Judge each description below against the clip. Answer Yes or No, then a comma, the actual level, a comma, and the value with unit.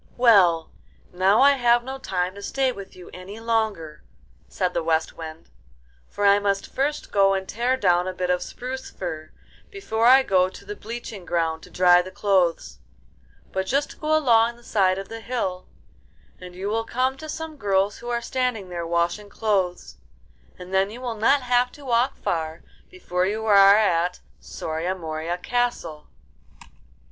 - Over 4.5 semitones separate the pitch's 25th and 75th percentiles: Yes, average, 5.1 semitones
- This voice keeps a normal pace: Yes, average, 175 wpm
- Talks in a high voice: Yes, high, 200 Hz